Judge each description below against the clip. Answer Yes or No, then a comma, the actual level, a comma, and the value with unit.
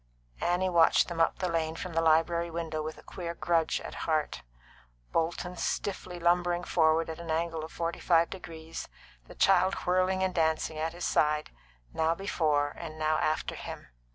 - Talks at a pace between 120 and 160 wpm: No, average, 180 wpm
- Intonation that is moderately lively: No, narrow, 1.7 semitones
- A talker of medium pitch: Yes, medium, 165 Hz